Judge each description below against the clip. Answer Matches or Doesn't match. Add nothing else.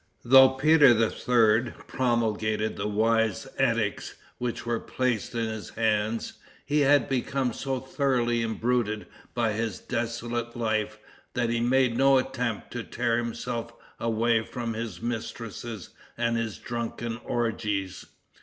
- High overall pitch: Doesn't match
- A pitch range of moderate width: Doesn't match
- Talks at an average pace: Doesn't match